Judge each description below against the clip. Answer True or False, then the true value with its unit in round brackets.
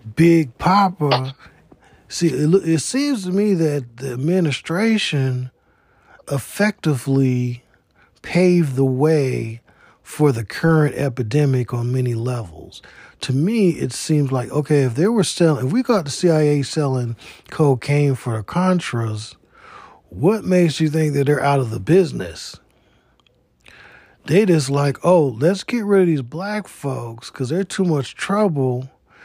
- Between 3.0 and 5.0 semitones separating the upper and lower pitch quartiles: False (5.5 semitones)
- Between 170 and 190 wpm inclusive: False (140 wpm)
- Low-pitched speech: False (145 Hz)